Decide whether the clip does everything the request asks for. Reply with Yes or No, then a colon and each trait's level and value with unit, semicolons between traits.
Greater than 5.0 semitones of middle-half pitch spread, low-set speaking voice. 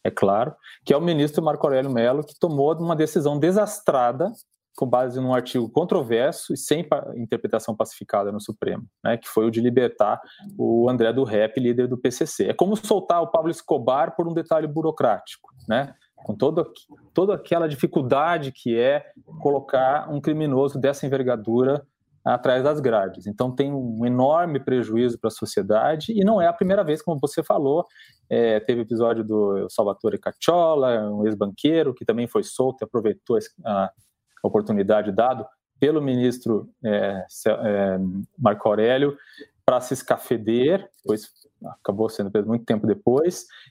Yes: wide, 5.5 semitones; low, 130 Hz